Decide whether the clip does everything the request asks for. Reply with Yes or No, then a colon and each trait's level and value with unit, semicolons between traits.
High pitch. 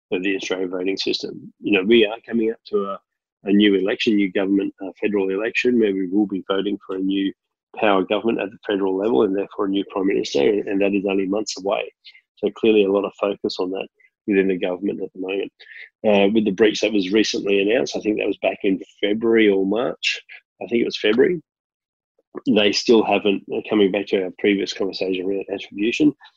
No: low, 100 Hz